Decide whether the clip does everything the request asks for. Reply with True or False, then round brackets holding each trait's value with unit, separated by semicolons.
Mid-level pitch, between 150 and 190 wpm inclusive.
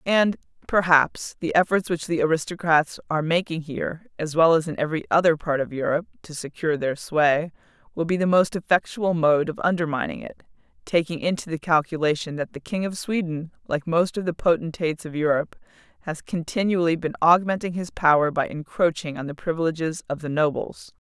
True (165 Hz; 175 wpm)